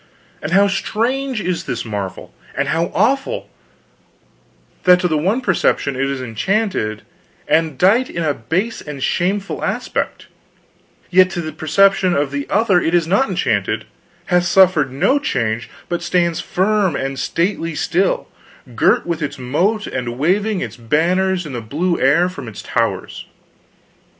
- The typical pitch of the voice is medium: Yes, medium, 175 Hz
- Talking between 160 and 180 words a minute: No, average, 150 wpm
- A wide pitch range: Yes, wide, 5.7 semitones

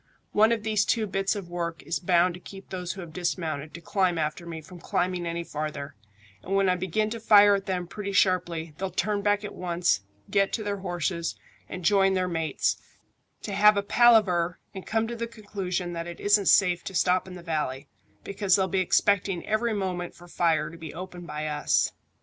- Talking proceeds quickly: Yes, fast, 210 wpm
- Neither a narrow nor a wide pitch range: Yes, average, 3.0 semitones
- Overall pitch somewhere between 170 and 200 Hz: Yes, medium, 185 Hz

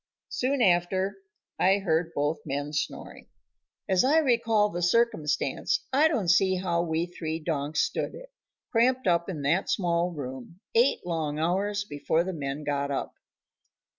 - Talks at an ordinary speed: Yes, average, 150 wpm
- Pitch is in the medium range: Yes, medium, 175 Hz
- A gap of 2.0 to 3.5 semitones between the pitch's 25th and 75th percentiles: No, average, 5.0 semitones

